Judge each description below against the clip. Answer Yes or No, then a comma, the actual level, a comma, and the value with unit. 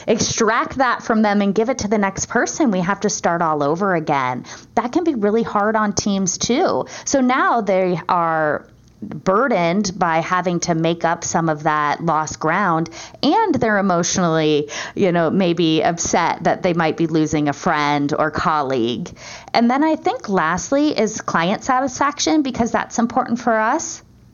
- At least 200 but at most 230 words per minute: No, average, 175 wpm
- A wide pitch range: Yes, wide, 6.2 semitones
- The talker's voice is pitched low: No, high, 195 Hz